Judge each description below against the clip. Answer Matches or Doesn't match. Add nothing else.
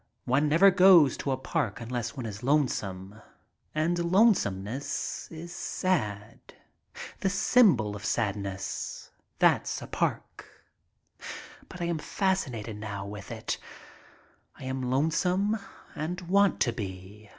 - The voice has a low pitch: Matches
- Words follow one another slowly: Matches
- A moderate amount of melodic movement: Doesn't match